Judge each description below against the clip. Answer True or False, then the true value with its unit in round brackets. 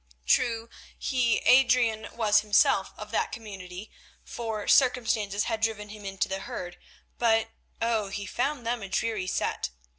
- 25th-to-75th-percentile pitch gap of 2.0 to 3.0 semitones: True (2.6 semitones)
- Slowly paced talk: False (145 wpm)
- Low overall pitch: False (220 Hz)